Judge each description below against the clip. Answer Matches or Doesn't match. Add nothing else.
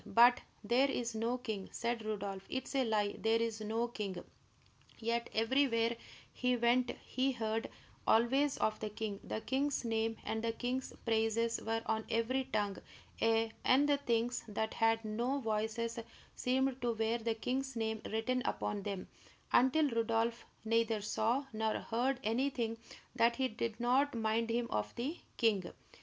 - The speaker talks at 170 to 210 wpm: Doesn't match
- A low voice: Doesn't match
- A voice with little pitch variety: Matches